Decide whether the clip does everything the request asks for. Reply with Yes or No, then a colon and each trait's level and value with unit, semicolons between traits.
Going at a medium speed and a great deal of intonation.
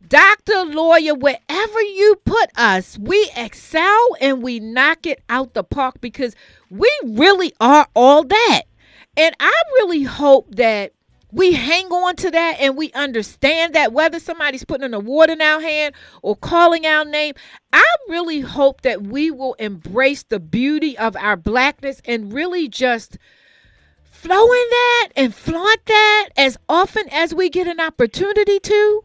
Yes: average, 155 wpm; wide, 5.7 semitones